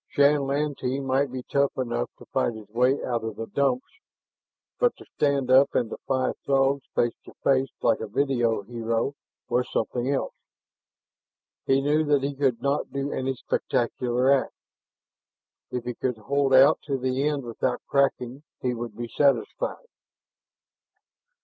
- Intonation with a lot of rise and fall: No, narrow, 2.5 semitones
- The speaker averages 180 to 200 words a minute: No, average, 155 wpm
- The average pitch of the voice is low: Yes, low, 130 Hz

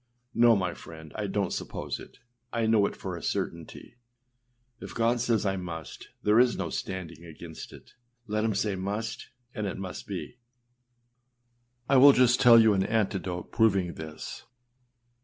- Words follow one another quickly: No, average, 165 wpm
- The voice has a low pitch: Yes, low, 100 Hz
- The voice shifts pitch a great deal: No, average, 4.1 semitones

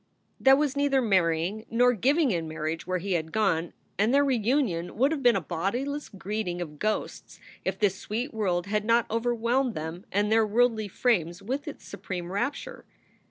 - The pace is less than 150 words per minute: No, average, 175 wpm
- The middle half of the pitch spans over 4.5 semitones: Yes, wide, 5.6 semitones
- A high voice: Yes, high, 215 Hz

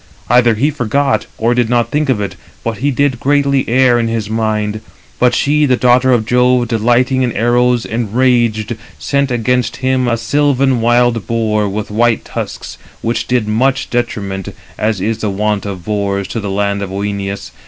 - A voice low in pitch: Yes, low, 120 Hz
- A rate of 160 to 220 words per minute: Yes, average, 175 wpm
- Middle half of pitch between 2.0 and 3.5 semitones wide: Yes, average, 2.9 semitones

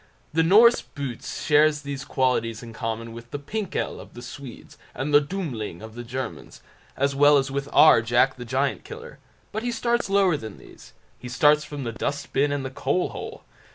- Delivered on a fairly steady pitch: No, average, 3.8 semitones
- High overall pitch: No, medium, 140 Hz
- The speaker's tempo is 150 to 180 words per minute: No, average, 190 wpm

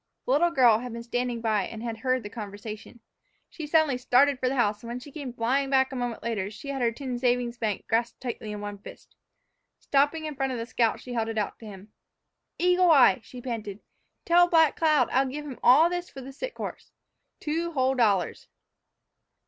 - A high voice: Yes, very high, 250 Hz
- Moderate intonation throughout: Yes, average, 3.7 semitones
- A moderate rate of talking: No, fast, 215 wpm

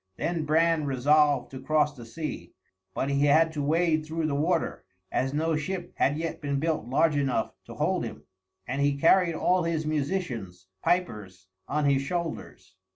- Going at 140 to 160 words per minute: No, average, 170 wpm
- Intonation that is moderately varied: Yes, average, 3.1 semitones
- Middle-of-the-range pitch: Yes, medium, 150 Hz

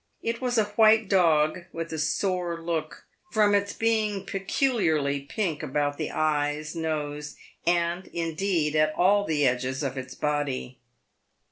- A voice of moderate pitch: Yes, medium, 165 Hz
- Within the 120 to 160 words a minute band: Yes, average, 145 wpm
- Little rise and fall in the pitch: No, average, 4.9 semitones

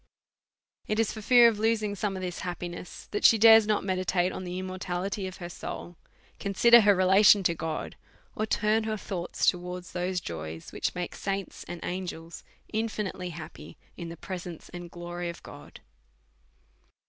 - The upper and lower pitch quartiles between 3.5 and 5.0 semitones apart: No, average, 2.9 semitones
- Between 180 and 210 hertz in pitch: Yes, medium, 185 Hz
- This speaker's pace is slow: No, average, 170 wpm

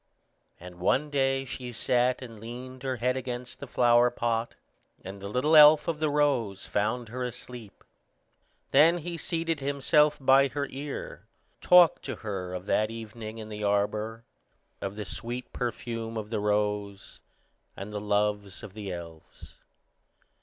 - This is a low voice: Yes, low, 120 Hz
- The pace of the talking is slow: No, average, 155 wpm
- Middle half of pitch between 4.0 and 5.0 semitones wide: Yes, average, 4.3 semitones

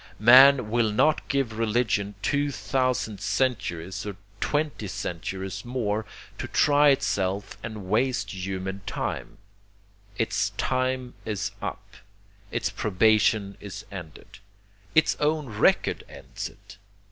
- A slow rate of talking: Yes, slow, 110 wpm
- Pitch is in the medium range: No, low, 110 Hz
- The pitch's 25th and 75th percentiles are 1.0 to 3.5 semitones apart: No, average, 4.8 semitones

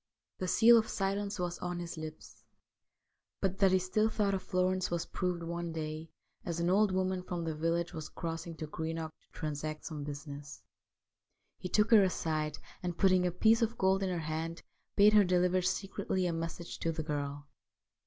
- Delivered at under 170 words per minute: No, average, 185 wpm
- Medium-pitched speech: Yes, medium, 175 Hz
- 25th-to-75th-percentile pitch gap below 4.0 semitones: Yes, average, 2.8 semitones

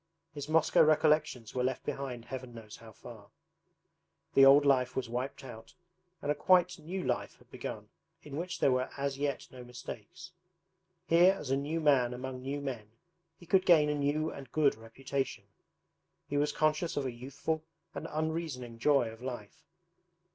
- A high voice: No, medium, 140 Hz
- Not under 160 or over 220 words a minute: Yes, average, 170 wpm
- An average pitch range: Yes, average, 3.7 semitones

